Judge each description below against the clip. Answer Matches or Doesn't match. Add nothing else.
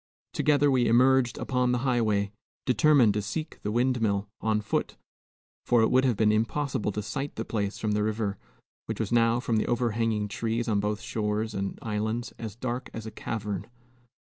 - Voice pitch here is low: Matches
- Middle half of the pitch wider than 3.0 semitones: Doesn't match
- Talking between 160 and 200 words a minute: Matches